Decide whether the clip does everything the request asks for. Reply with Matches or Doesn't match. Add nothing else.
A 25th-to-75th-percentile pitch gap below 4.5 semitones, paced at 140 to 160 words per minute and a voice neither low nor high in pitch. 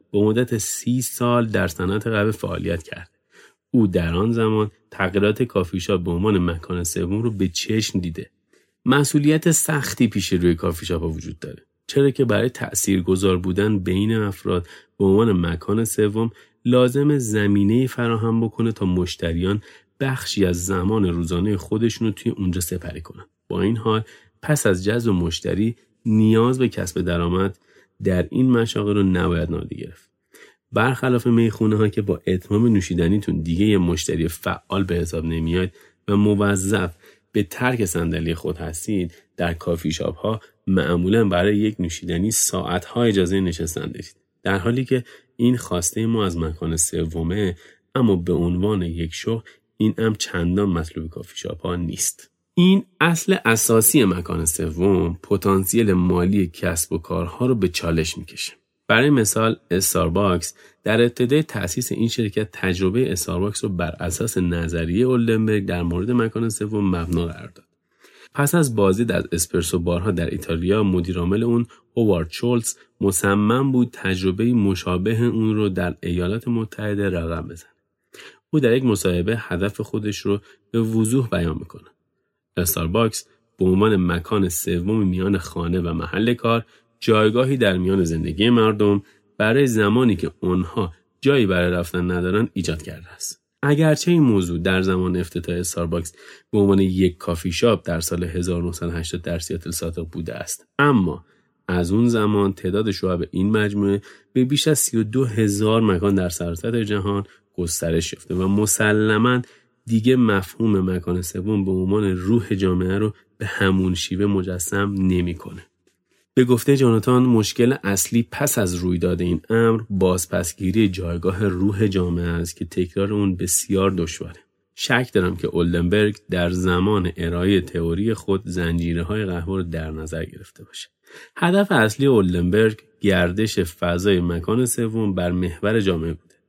Doesn't match